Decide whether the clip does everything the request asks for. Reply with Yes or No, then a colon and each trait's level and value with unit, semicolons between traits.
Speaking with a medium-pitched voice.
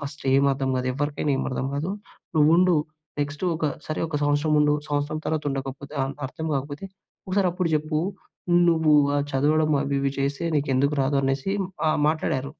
Yes: medium, 145 Hz